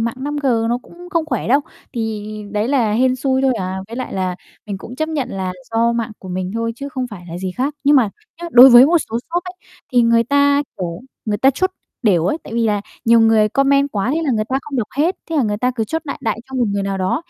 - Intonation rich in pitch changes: No, average, 4.7 semitones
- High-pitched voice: Yes, high, 235 Hz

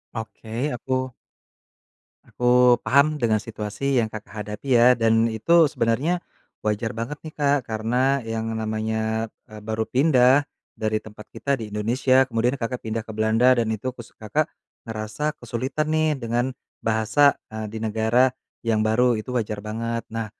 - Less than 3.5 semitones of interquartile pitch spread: Yes, average, 2.8 semitones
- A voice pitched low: Yes, low, 115 Hz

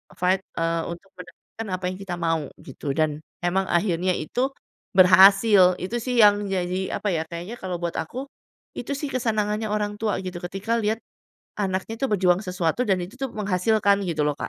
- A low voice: No, high, 190 Hz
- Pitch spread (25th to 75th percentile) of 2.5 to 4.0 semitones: Yes, average, 3.2 semitones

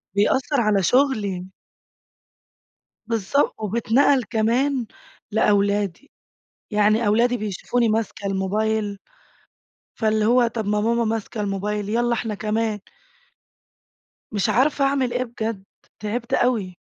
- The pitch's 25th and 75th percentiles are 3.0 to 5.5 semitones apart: No, narrow, 2.6 semitones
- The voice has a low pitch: No, high, 220 Hz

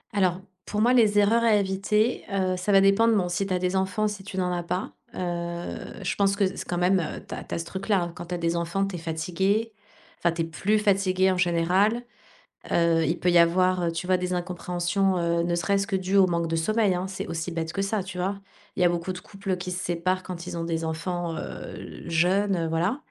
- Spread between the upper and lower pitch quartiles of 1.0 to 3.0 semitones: Yes, narrow, 2.4 semitones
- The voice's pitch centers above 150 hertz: Yes, medium, 185 Hz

